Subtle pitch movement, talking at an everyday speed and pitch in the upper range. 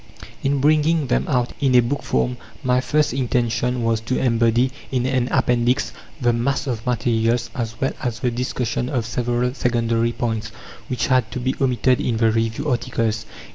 No: narrow, 2.1 semitones; average, 175 wpm; low, 120 Hz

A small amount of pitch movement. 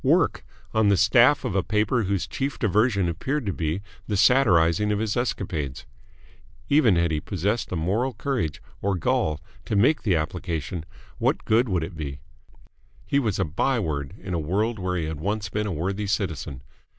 No: average, 5.0 semitones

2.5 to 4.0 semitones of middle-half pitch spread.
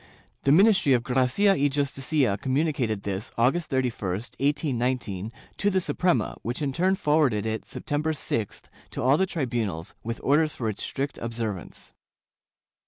No: average, 4.8 semitones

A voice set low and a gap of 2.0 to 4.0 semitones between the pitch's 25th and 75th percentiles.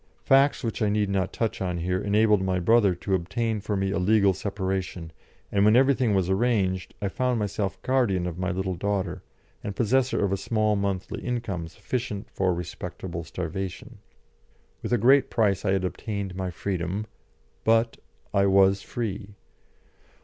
Yes: low, 100 Hz; average, 2.8 semitones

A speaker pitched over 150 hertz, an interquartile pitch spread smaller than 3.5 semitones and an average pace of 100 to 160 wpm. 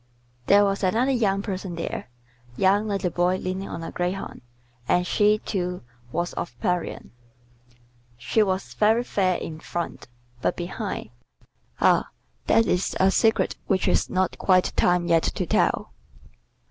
Yes: medium, 185 Hz; narrow, 2.4 semitones; average, 145 wpm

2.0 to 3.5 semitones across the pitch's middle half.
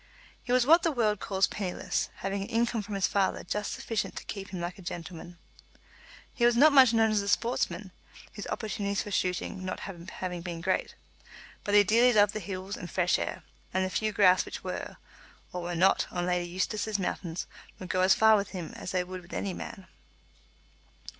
Yes: average, 2.9 semitones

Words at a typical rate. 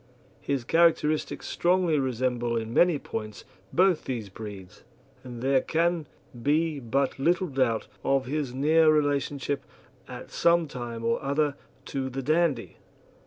No: slow, 130 wpm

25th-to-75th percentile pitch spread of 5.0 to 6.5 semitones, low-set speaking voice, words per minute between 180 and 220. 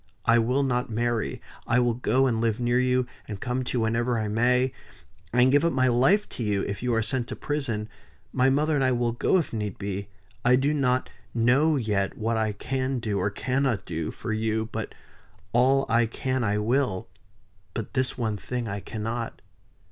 No: average, 2.7 semitones; low, 120 Hz; average, 200 wpm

